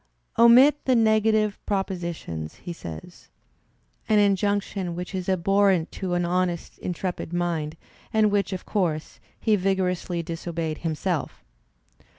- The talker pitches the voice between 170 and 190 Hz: Yes, medium, 185 Hz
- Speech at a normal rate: No, slow, 125 wpm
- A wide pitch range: No, average, 3.2 semitones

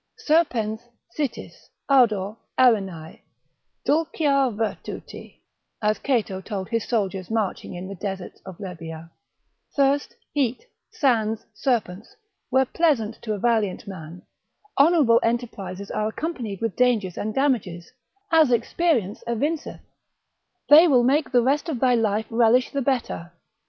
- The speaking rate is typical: No, slow, 125 wpm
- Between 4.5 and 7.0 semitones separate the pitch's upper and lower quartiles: Yes, average, 5.3 semitones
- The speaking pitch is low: No, high, 230 Hz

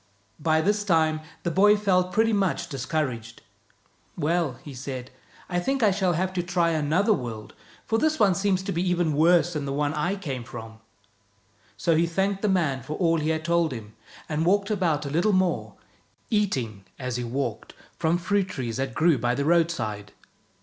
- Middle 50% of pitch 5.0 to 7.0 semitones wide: Yes, wide, 5.4 semitones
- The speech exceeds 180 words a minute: Yes, average, 190 wpm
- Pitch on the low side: No, medium, 165 Hz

